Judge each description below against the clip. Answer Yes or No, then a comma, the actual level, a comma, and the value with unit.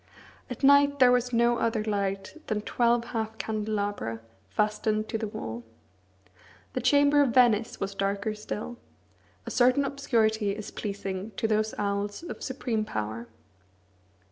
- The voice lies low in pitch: No, high, 220 Hz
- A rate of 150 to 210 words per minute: No, average, 140 wpm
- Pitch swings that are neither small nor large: Yes, average, 3.1 semitones